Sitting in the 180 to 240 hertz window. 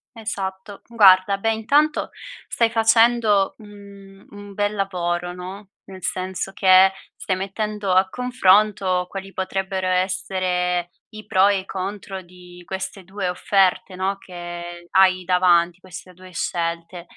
Yes: high, 190 Hz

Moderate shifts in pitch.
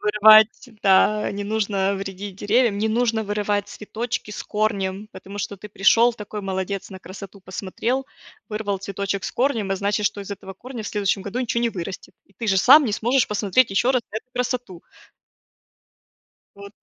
No: narrow, 2.2 semitones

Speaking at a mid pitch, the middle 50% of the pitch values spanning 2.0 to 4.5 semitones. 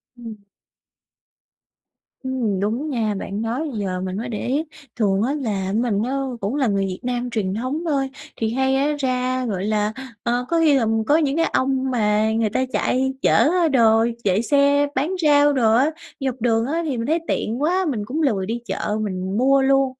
No: high, 245 Hz; average, 4.2 semitones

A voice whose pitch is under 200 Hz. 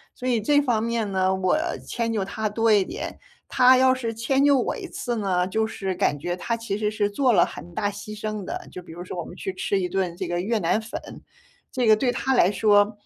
No: high, 215 Hz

